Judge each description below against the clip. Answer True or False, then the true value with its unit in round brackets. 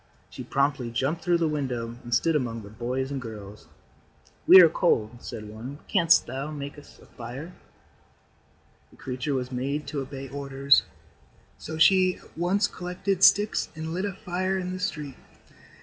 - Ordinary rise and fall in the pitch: False (5.7 semitones)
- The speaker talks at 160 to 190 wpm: True (170 wpm)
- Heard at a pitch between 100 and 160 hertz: True (140 Hz)